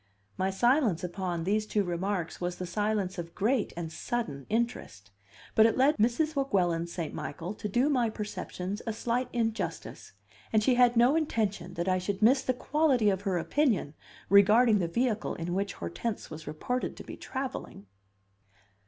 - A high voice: Yes, high, 210 Hz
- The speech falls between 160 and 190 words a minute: Yes, average, 170 wpm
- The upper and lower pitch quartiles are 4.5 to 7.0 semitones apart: Yes, average, 5.2 semitones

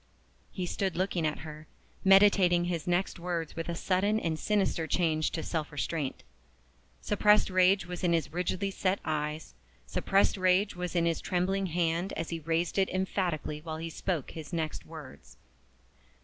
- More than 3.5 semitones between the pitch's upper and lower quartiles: No, average, 2.8 semitones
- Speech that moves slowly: No, average, 165 wpm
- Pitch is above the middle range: No, medium, 175 Hz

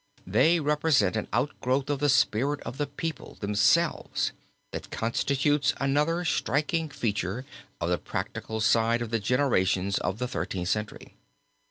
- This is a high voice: No, low, 125 Hz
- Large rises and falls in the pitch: Yes, wide, 5.7 semitones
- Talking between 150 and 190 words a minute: No, average, 140 wpm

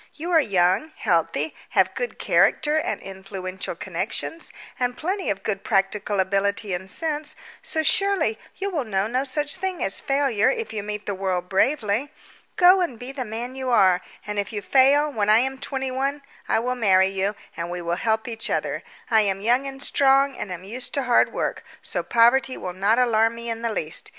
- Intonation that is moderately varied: No, wide, 5.9 semitones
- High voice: Yes, high, 230 Hz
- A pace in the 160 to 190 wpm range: No, average, 200 wpm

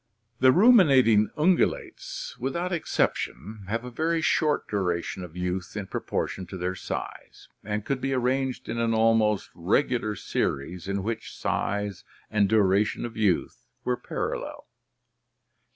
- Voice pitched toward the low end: Yes, low, 110 Hz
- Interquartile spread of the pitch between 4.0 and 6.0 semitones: Yes, average, 5.2 semitones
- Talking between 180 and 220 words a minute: No, slow, 135 wpm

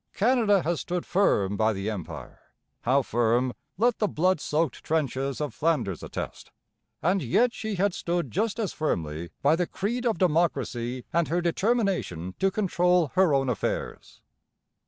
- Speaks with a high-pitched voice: No, medium, 165 Hz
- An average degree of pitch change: No, wide, 7.3 semitones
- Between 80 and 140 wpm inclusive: No, average, 155 wpm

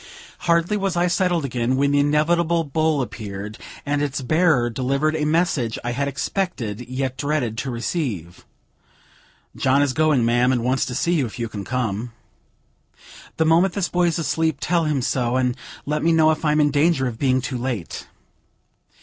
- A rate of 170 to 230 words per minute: Yes, average, 185 wpm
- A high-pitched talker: No, medium, 140 Hz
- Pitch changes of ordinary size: Yes, average, 4.6 semitones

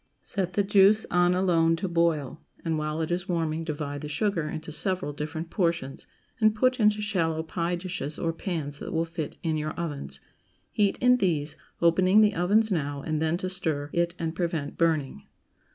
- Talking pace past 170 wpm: Yes, average, 185 wpm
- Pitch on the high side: No, medium, 165 Hz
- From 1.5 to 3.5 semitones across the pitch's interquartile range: Yes, average, 3.2 semitones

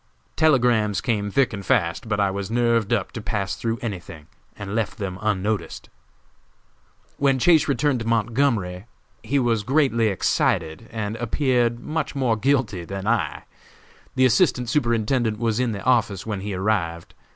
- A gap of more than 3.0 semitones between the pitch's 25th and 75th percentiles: Yes, average, 3.5 semitones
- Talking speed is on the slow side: No, average, 150 wpm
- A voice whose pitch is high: No, low, 115 Hz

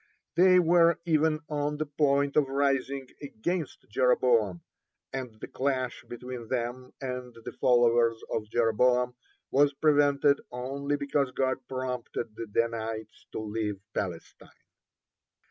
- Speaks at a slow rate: Yes, slow, 120 wpm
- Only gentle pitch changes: No, average, 3.5 semitones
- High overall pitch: No, low, 130 Hz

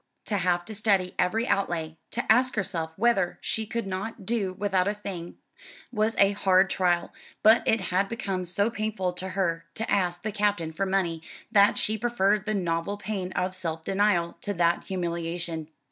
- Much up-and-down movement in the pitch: No, average, 3.2 semitones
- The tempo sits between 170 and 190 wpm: Yes, average, 175 wpm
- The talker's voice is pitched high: Yes, high, 195 Hz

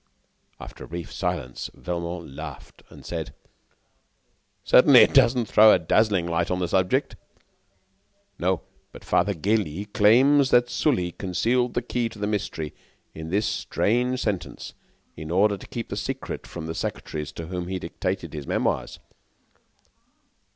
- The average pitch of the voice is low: Yes, very low, 95 Hz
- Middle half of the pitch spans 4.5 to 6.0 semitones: Yes, average, 5.2 semitones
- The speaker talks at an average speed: Yes, average, 150 wpm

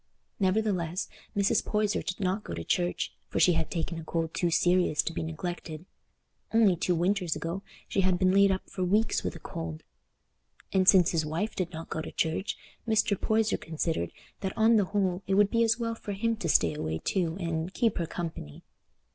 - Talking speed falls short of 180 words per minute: No, average, 200 wpm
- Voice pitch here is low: No, medium, 185 Hz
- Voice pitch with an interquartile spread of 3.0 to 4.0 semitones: Yes, average, 3.7 semitones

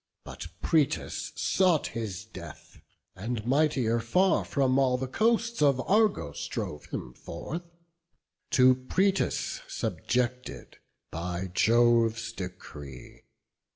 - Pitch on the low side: Yes, low, 125 Hz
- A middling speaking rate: No, slow, 100 wpm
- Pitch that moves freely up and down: Yes, wide, 6.8 semitones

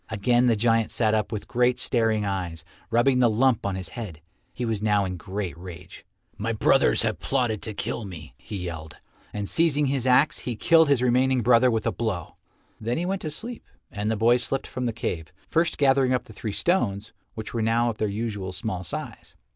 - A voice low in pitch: Yes, low, 115 Hz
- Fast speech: Yes, fast, 210 wpm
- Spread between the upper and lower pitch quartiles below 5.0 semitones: Yes, average, 3.9 semitones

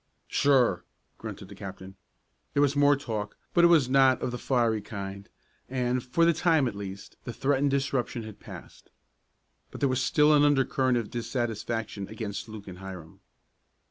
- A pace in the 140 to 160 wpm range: No, average, 170 wpm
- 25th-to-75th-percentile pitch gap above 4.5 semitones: Yes, average, 5.1 semitones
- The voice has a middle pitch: No, low, 120 Hz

